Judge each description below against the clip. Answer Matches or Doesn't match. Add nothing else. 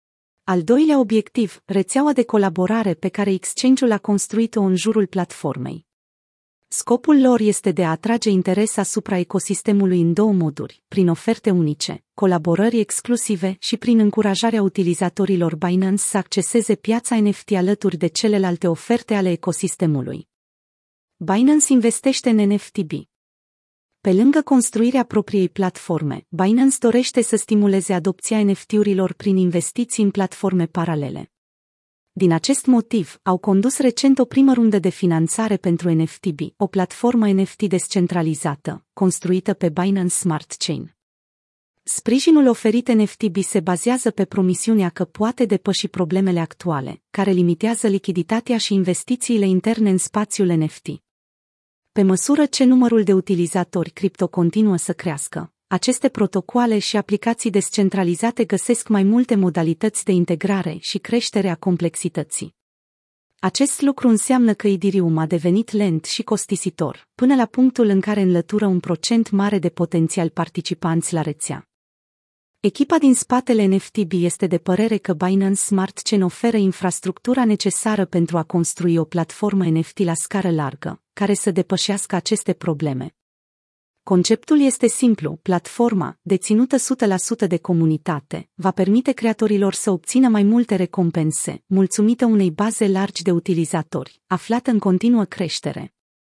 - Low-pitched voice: Doesn't match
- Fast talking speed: Doesn't match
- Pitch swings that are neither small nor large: Matches